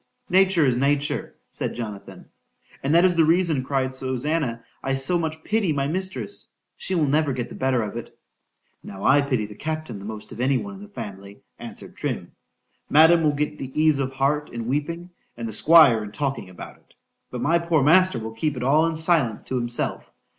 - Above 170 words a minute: Yes, average, 185 wpm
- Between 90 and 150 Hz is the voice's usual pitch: Yes, medium, 140 Hz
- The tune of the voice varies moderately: Yes, average, 5.0 semitones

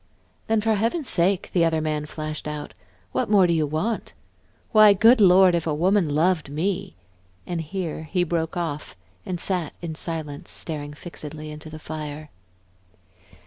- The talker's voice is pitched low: No, medium, 165 Hz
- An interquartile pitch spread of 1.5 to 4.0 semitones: Yes, average, 3.5 semitones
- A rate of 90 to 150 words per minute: No, average, 160 wpm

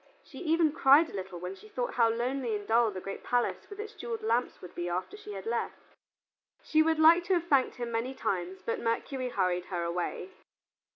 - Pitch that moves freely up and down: Yes, wide, 7.9 semitones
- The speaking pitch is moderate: No, high, 235 Hz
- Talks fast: Yes, fast, 215 wpm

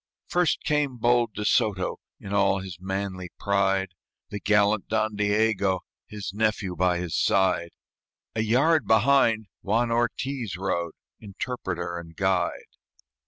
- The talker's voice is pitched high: No, low, 100 Hz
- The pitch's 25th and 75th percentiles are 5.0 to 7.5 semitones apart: No, average, 3.0 semitones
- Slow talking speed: Yes, slow, 130 wpm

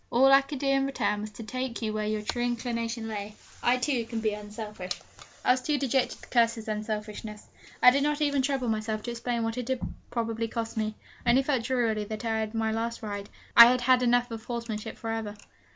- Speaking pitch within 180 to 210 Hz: No, high, 230 Hz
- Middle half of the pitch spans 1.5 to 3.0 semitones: Yes, narrow, 2.6 semitones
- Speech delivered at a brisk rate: Yes, fast, 230 wpm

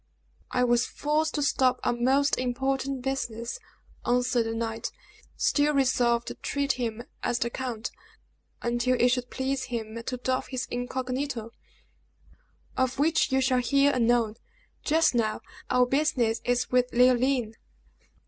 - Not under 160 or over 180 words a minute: No, average, 140 wpm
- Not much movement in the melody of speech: Yes, narrow, 2.1 semitones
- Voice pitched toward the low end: No, very high, 250 Hz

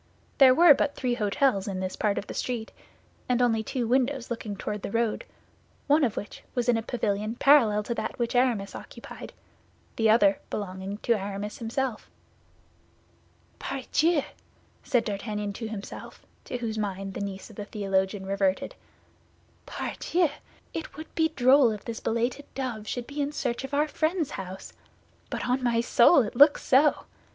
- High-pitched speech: Yes, high, 235 Hz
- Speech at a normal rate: Yes, average, 165 wpm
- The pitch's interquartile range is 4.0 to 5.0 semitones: Yes, average, 4.5 semitones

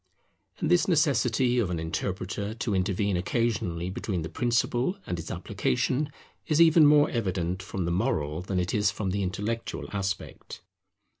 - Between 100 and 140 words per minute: No, average, 155 wpm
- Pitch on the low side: Yes, low, 100 Hz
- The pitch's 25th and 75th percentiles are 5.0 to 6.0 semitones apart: Yes, average, 5.3 semitones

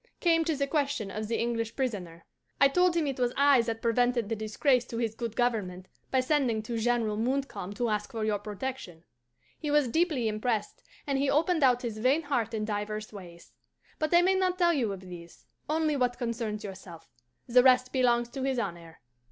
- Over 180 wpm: Yes, average, 200 wpm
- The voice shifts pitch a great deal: No, average, 4.5 semitones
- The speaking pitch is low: No, high, 240 Hz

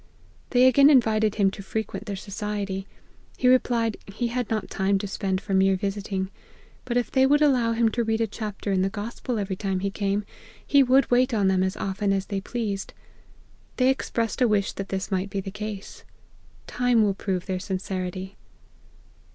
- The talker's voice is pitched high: Yes, high, 205 Hz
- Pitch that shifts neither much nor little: Yes, average, 3.3 semitones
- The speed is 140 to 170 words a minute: No, average, 190 wpm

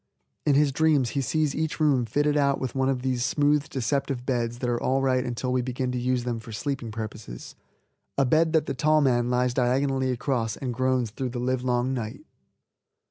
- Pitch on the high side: No, low, 130 Hz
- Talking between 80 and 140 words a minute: No, average, 200 wpm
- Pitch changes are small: Yes, narrow, 2.3 semitones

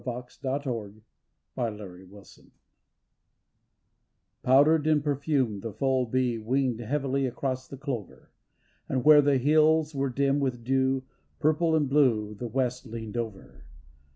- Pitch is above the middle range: No, low, 130 Hz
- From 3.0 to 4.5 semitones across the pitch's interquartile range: Yes, average, 3.5 semitones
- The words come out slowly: Yes, slow, 125 wpm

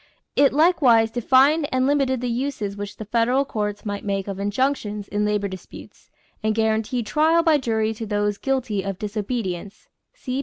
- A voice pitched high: Yes, high, 225 Hz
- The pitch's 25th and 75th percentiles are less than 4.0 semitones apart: No, average, 4.3 semitones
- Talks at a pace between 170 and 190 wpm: Yes, average, 175 wpm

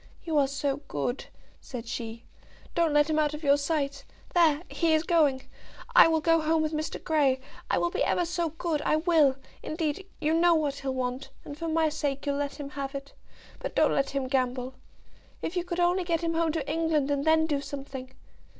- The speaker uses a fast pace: Yes, fast, 210 wpm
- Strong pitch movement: No, average, 2.9 semitones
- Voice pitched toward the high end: Yes, very high, 300 Hz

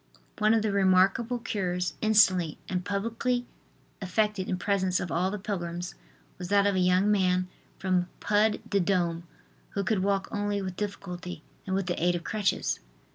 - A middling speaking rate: Yes, average, 170 wpm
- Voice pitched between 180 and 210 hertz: Yes, high, 190 Hz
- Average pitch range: No, narrow, 2.3 semitones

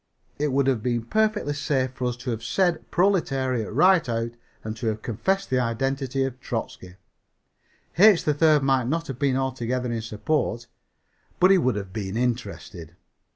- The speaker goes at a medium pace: Yes, average, 165 wpm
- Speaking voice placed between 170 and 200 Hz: No, low, 130 Hz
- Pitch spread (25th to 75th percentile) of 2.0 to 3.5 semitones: No, average, 4.3 semitones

